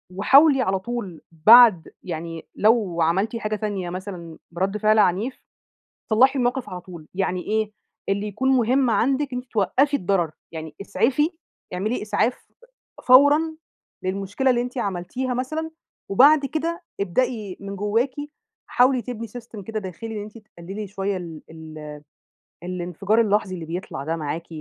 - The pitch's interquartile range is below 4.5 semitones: No, wide, 5.4 semitones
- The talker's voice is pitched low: No, high, 210 Hz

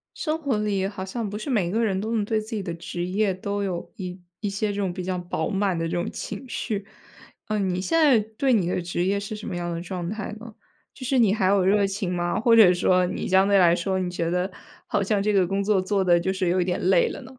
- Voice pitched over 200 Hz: No, high, 195 Hz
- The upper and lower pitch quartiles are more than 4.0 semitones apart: No, average, 2.7 semitones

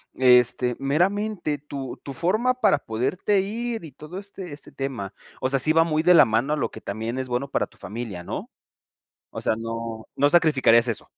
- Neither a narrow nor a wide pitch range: No, wide, 6.4 semitones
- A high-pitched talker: No, medium, 140 Hz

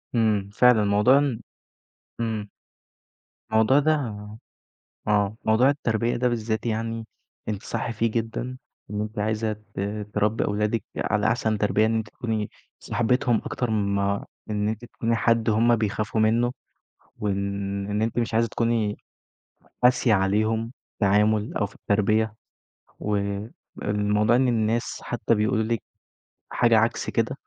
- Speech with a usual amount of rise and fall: No, narrow, 1.8 semitones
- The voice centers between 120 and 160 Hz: No, low, 110 Hz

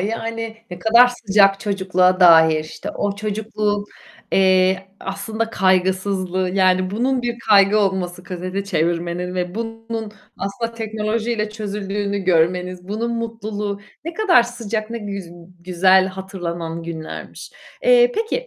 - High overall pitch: Yes, high, 200 Hz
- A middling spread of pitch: Yes, average, 3.3 semitones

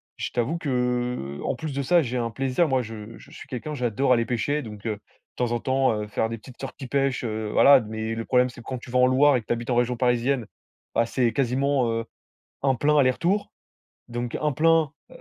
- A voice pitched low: Yes, low, 125 Hz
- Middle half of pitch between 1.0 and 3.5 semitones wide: Yes, average, 2.8 semitones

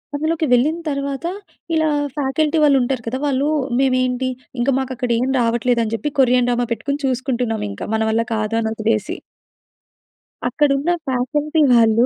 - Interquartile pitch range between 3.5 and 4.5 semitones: No, average, 3.1 semitones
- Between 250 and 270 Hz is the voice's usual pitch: Yes, very high, 255 Hz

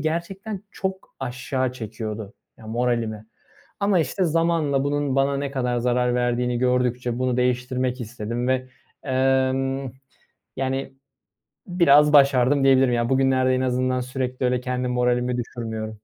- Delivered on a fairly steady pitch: Yes, narrow, 1.8 semitones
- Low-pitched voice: Yes, low, 130 Hz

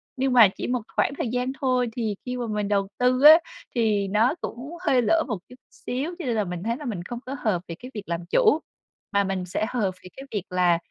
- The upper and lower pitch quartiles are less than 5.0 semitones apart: Yes, average, 4.1 semitones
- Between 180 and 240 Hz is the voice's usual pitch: Yes, high, 235 Hz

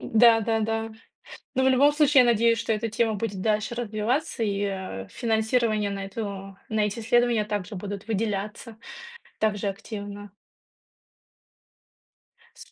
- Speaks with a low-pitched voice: No, high, 220 Hz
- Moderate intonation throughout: No, narrow, 2.2 semitones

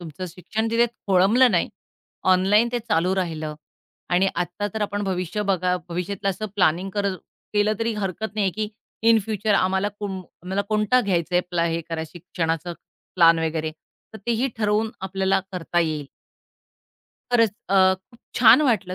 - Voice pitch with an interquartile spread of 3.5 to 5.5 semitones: No, average, 3.1 semitones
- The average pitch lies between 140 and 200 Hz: Yes, high, 190 Hz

